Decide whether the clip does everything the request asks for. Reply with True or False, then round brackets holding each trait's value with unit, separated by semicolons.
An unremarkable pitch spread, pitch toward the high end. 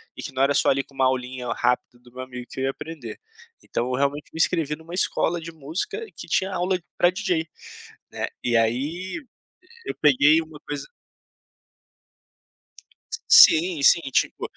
False (4.7 semitones; 150 Hz)